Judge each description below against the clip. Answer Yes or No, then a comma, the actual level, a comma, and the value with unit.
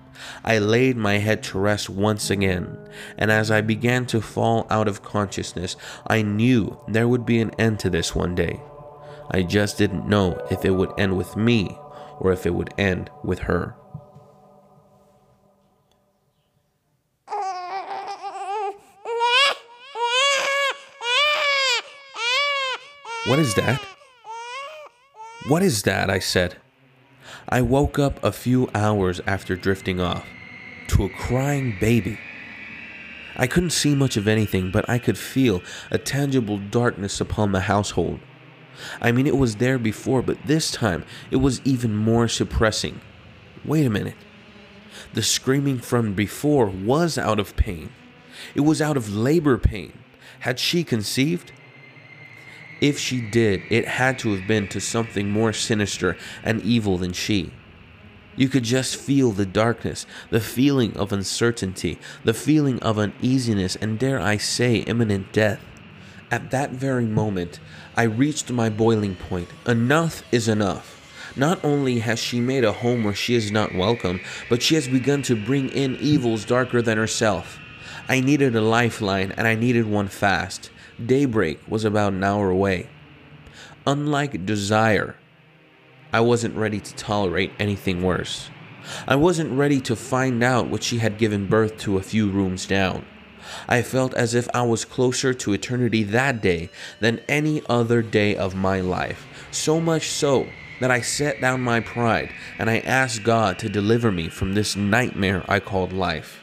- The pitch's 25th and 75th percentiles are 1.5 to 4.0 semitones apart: No, average, 5.3 semitones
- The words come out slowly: No, average, 150 wpm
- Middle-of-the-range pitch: No, low, 115 Hz